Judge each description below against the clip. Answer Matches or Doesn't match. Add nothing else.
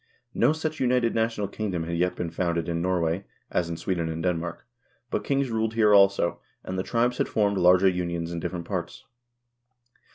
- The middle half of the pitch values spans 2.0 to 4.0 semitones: Doesn't match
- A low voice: Matches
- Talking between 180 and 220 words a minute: Matches